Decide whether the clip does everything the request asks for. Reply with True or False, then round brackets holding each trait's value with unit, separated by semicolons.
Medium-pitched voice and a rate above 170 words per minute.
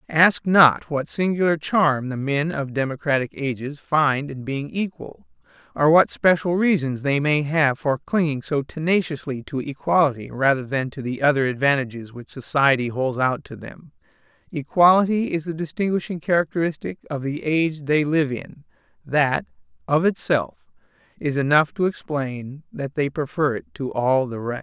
False (150 Hz; 160 wpm)